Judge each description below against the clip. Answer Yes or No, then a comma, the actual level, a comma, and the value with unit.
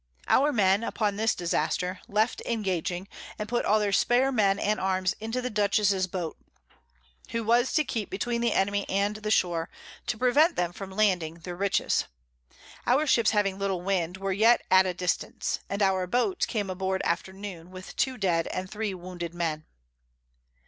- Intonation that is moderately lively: Yes, average, 3.1 semitones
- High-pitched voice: Yes, high, 195 Hz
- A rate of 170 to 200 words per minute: Yes, average, 175 wpm